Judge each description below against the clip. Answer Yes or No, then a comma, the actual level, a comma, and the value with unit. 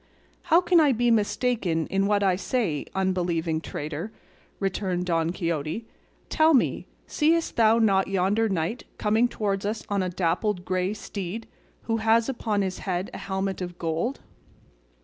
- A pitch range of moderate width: Yes, average, 4.0 semitones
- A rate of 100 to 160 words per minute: Yes, average, 150 wpm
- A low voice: No, high, 195 Hz